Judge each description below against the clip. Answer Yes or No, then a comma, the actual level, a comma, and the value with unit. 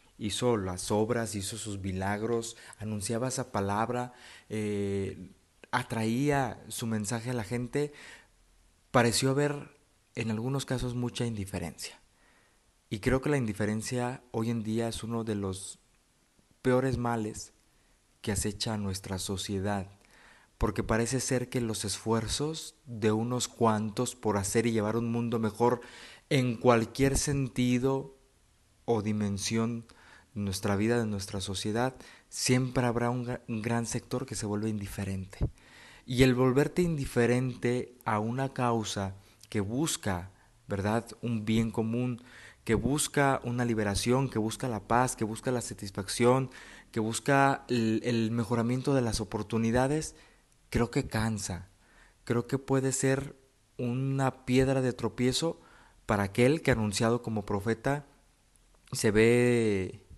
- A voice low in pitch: Yes, low, 115 Hz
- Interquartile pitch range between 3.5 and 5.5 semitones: No, average, 2.9 semitones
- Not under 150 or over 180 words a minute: No, average, 130 wpm